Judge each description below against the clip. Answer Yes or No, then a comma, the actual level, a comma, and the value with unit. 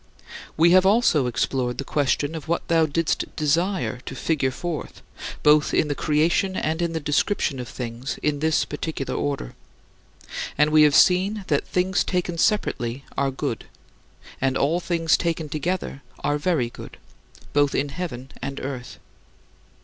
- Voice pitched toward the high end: No, medium, 150 Hz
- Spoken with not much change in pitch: No, average, 3.7 semitones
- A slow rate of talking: No, average, 155 wpm